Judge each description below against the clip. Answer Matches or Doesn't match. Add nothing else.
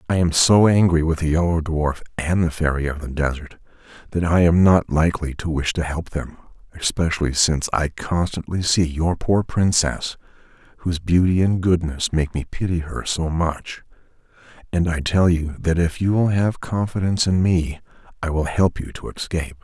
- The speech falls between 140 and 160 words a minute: Doesn't match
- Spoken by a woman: Doesn't match